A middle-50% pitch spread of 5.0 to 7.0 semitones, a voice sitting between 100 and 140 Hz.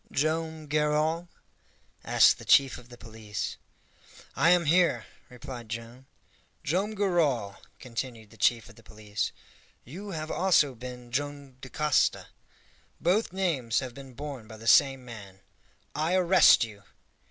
Yes: wide, 5.4 semitones; low, 135 Hz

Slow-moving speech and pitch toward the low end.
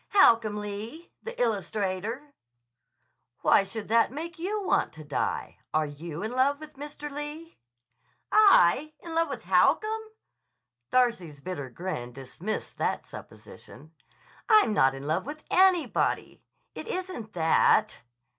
No: slow, 125 wpm; high, 230 Hz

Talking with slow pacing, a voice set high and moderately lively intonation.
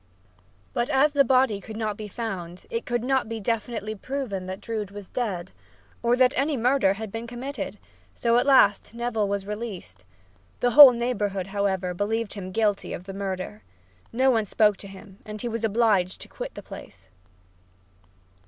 No: average, 175 wpm; high, 220 Hz; average, 3.4 semitones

